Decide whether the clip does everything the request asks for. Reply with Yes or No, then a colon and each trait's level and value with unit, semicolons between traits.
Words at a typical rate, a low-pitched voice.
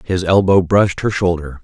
Yes: average, 185 wpm; very low, 90 Hz